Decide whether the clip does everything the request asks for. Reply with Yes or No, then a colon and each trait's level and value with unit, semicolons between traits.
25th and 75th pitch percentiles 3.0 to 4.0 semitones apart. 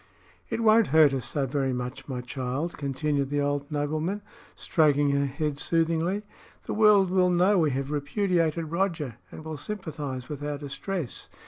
Yes: average, 3.7 semitones